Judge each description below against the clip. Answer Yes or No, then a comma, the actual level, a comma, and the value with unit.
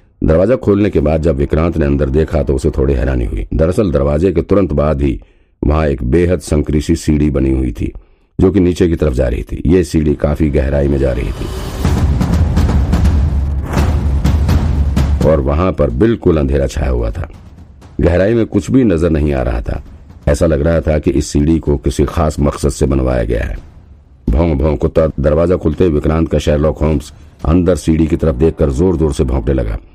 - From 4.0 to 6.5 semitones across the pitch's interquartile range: No, average, 2.8 semitones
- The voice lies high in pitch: No, very low, 75 Hz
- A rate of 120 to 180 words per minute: No, fast, 190 wpm